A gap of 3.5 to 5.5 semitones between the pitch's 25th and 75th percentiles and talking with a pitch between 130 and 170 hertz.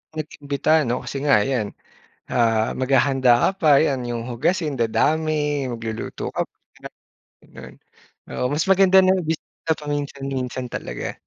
Yes: average, 4.1 semitones; medium, 140 Hz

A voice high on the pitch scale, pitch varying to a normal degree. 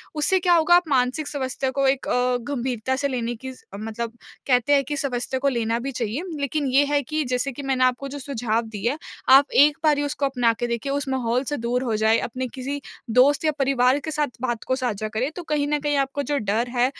Yes: very high, 265 Hz; average, 3.0 semitones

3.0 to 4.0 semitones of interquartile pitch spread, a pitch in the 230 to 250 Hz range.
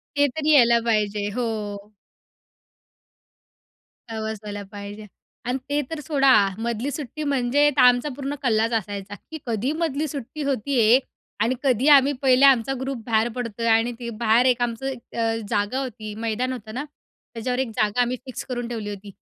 Yes: average, 3.4 semitones; high, 245 Hz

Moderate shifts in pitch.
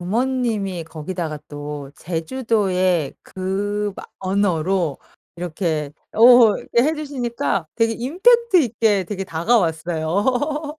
No: wide, 6.4 semitones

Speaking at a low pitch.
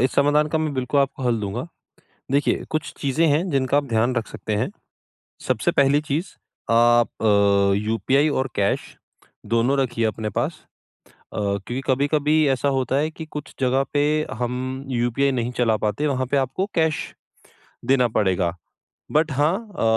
Yes: low, 130 Hz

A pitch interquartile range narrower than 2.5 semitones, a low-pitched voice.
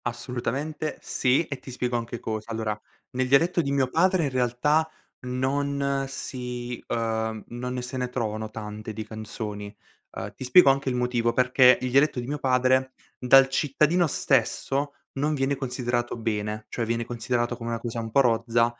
No: average, 2.8 semitones; low, 125 Hz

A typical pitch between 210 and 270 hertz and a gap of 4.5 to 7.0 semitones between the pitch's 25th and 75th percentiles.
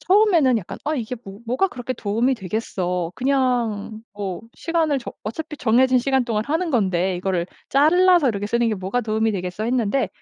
Yes: high, 235 Hz; average, 5.1 semitones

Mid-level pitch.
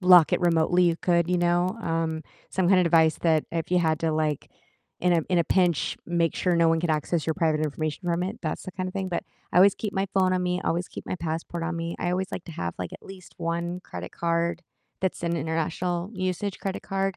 Yes: medium, 170 Hz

